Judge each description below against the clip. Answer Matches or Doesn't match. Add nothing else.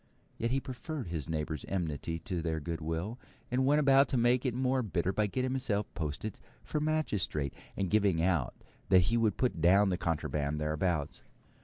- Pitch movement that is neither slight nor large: Doesn't match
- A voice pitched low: Matches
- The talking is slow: Doesn't match